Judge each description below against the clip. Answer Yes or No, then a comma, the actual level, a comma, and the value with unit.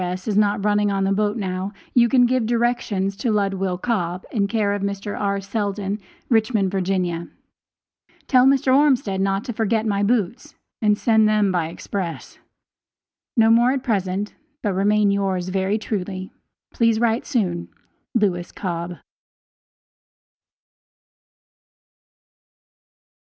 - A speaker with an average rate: No, slow, 130 wpm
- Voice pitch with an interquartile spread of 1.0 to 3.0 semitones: Yes, average, 2.7 semitones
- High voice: Yes, high, 205 Hz